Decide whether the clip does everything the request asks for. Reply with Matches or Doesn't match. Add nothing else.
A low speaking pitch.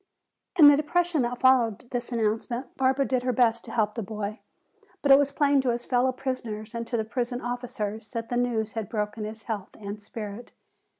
Doesn't match